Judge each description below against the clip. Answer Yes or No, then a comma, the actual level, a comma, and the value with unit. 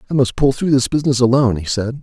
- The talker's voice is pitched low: Yes, low, 125 Hz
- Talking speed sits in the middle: No, fast, 265 wpm